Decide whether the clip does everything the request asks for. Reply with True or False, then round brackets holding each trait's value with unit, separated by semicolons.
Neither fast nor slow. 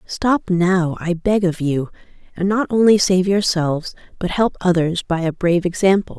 True (175 wpm)